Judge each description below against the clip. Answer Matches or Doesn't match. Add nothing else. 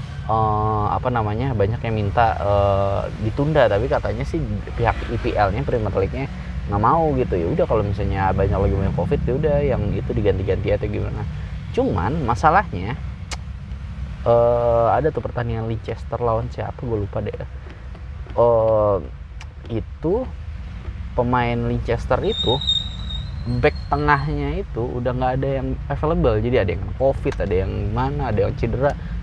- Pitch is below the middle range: Matches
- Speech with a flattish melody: Doesn't match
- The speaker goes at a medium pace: Doesn't match